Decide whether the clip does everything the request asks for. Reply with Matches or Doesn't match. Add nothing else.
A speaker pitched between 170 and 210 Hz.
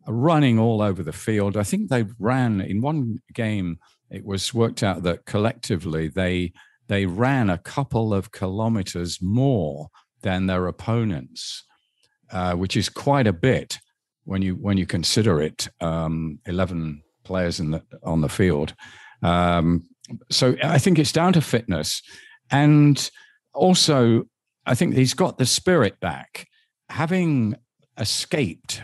Doesn't match